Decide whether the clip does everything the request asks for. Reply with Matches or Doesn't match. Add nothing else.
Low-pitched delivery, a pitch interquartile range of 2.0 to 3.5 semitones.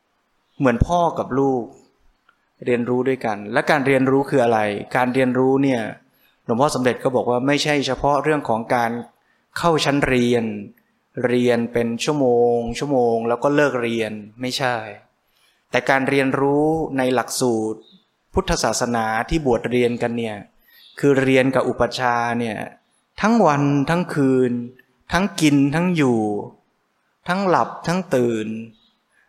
Matches